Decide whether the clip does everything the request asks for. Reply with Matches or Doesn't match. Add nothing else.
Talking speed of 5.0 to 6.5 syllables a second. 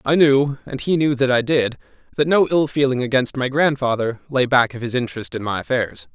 Matches